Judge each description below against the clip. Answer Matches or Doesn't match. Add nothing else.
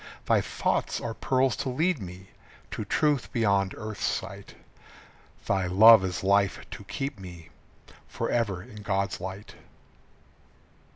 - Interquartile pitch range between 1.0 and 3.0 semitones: Doesn't match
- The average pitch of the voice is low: Matches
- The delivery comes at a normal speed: Doesn't match